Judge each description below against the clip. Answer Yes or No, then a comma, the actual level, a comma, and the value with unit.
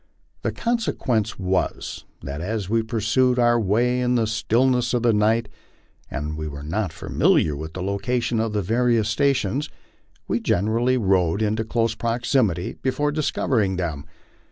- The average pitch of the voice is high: No, low, 110 Hz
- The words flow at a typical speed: Yes, average, 145 wpm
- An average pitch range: Yes, average, 4.2 semitones